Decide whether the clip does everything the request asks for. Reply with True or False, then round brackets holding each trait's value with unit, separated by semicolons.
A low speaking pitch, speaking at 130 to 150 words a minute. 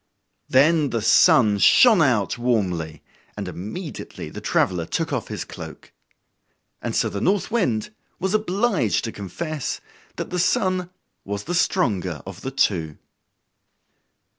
True (125 Hz; 135 wpm)